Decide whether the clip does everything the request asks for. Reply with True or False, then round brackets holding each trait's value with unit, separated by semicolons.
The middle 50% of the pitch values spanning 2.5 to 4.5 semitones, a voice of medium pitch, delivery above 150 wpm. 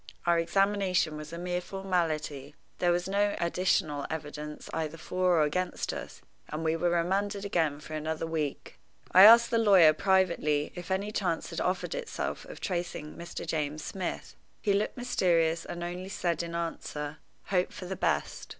True (3.2 semitones; 175 Hz; 170 wpm)